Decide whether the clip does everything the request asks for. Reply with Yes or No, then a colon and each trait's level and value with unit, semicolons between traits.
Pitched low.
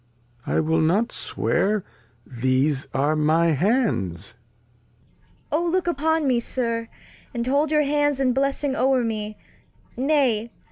No: high, 235 Hz